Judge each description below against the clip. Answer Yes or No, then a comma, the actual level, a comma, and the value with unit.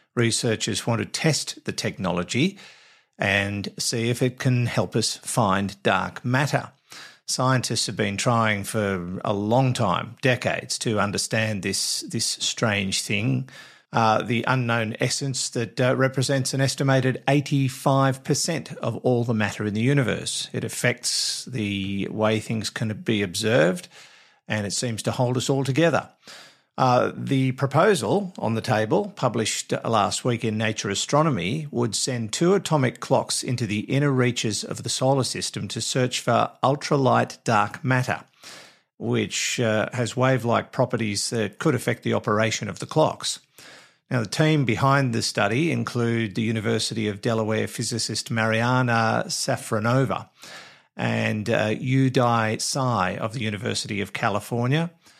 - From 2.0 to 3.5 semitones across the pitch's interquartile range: Yes, average, 3.1 semitones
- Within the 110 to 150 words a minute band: Yes, average, 140 wpm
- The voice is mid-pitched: No, low, 120 Hz